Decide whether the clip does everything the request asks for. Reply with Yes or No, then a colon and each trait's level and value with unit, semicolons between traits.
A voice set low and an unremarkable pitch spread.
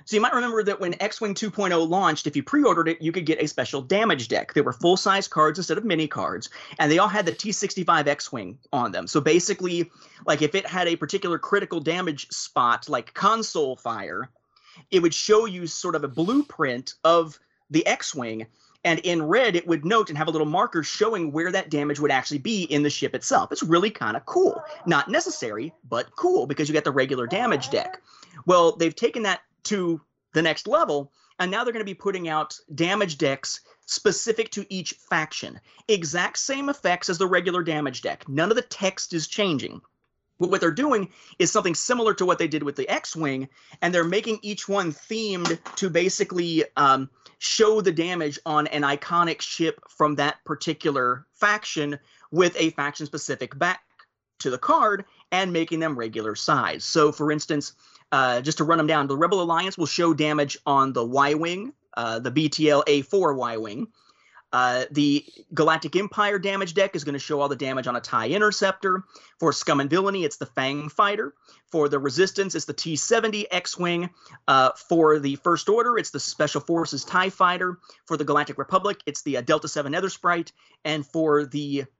No: medium, 165 Hz; average, 4.8 semitones